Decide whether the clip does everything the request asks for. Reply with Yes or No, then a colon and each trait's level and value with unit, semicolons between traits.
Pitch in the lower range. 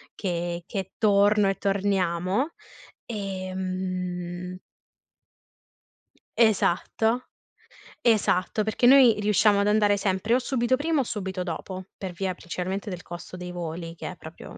No: high, 195 Hz